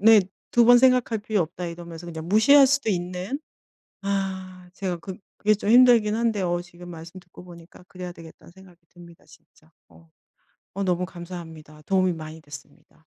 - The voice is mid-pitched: Yes, medium, 180 Hz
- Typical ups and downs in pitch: Yes, average, 3.5 semitones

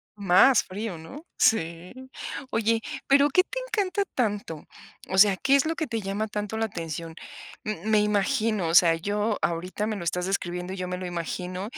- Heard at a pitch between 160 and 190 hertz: No, high, 205 Hz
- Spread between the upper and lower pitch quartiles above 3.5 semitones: Yes, average, 4.0 semitones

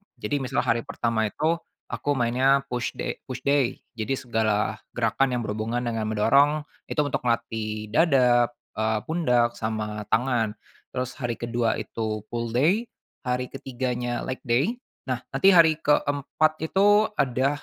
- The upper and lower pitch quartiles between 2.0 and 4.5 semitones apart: Yes, average, 3.8 semitones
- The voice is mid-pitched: No, low, 125 Hz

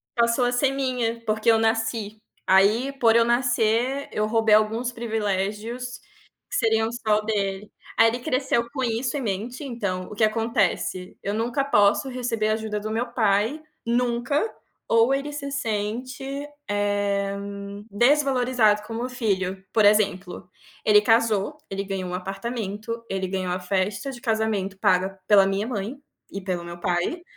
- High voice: Yes, high, 220 Hz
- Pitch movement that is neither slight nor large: Yes, average, 3.2 semitones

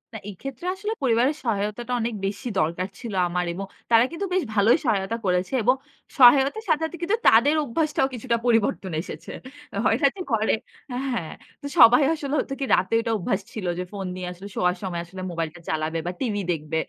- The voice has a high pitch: Yes, high, 225 Hz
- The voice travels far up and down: Yes, wide, 6.4 semitones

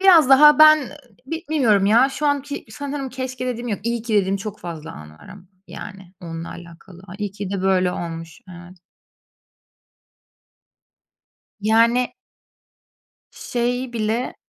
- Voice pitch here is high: Yes, high, 220 Hz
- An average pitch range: No, wide, 6.0 semitones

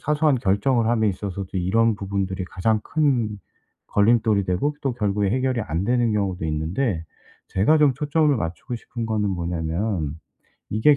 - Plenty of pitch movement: No, average, 4.7 semitones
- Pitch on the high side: No, low, 105 Hz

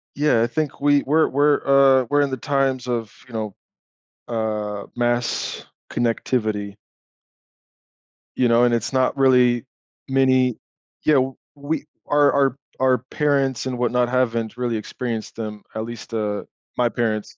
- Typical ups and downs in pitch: Yes, average, 3.0 semitones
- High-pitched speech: No, low, 125 Hz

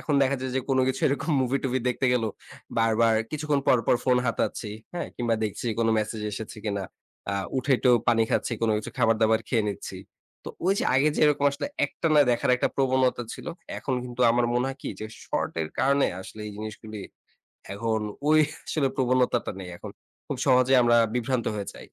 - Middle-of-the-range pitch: No, low, 125 Hz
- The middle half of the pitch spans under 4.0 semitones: Yes, average, 3.0 semitones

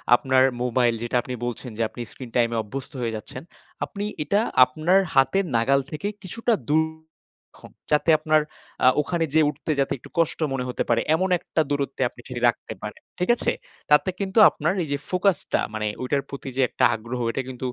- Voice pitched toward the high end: No, medium, 140 Hz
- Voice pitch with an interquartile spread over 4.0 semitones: Yes, average, 4.6 semitones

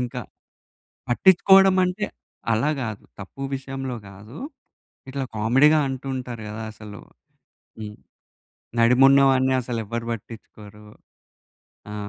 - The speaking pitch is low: Yes, low, 125 Hz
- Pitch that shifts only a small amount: No, average, 3.6 semitones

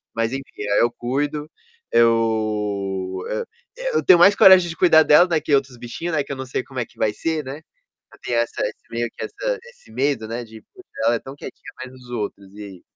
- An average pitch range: No, wide, 5.7 semitones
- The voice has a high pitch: No, low, 130 Hz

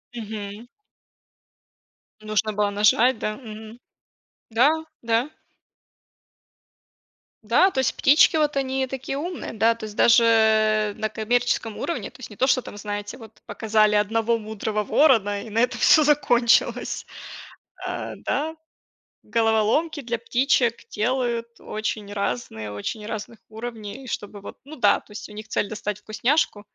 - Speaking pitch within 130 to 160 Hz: No, high, 225 Hz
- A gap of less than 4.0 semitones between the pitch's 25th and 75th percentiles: Yes, average, 2.8 semitones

